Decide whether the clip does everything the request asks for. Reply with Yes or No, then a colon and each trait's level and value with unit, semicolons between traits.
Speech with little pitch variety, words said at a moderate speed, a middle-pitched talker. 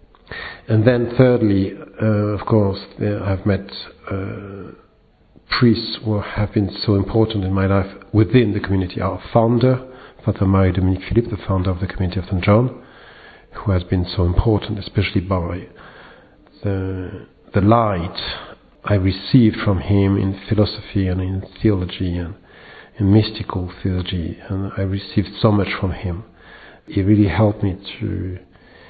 No: narrow, 2.3 semitones; average, 145 wpm; low, 100 Hz